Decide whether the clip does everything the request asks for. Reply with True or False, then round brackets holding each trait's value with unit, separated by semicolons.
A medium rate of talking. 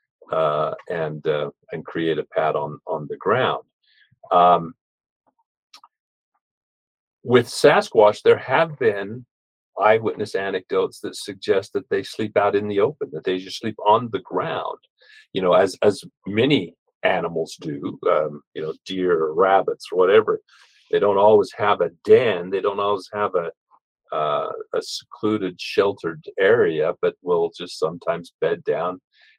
True (145 wpm)